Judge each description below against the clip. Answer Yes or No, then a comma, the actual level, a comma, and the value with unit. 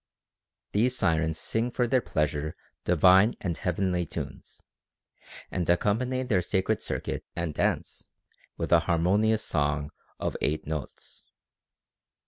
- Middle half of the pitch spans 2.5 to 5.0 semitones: No, wide, 5.5 semitones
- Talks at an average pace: No, slow, 115 wpm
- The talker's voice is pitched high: No, very low, 90 Hz